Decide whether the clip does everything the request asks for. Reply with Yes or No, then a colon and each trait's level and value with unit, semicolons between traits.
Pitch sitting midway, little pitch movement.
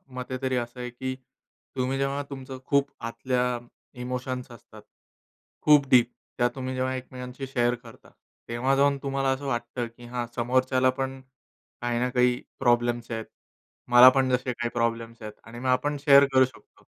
No: low, 125 Hz; narrow, 1.7 semitones